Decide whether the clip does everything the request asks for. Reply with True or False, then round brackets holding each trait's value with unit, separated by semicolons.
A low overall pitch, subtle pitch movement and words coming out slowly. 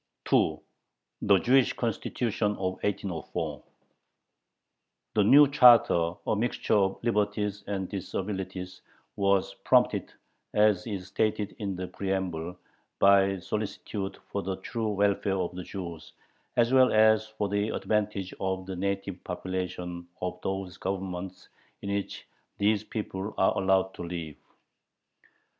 True (95 Hz; 2.1 semitones; 120 wpm)